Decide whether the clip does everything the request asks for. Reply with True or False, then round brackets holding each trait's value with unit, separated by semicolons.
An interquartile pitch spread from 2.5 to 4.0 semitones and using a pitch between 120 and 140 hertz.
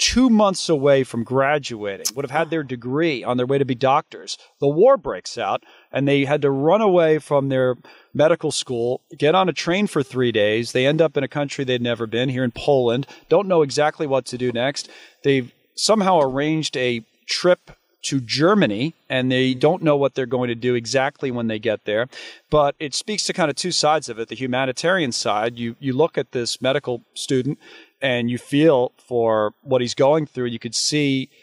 True (3.4 semitones; 135 Hz)